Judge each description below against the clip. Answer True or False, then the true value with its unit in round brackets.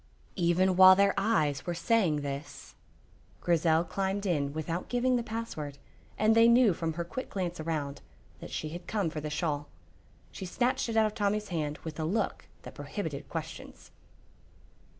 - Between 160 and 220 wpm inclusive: True (170 wpm)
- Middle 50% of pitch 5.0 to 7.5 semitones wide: True (5.5 semitones)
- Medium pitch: True (175 Hz)